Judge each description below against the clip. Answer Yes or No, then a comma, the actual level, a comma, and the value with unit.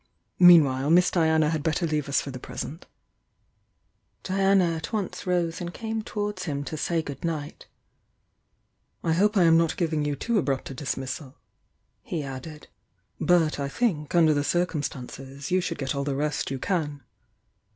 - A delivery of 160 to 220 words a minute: Yes, average, 175 wpm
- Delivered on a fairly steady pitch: No, average, 3.8 semitones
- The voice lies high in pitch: No, medium, 160 Hz